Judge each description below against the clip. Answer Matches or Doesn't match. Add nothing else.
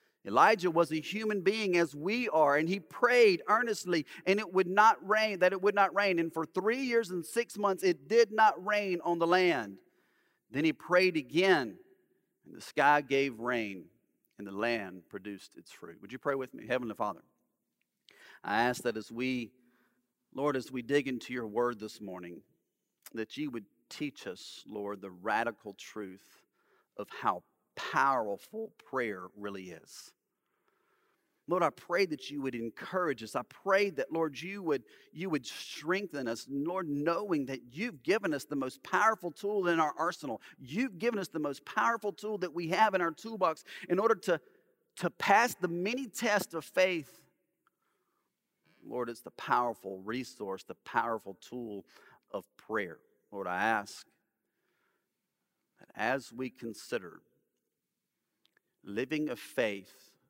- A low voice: Doesn't match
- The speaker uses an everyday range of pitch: Doesn't match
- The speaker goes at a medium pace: Matches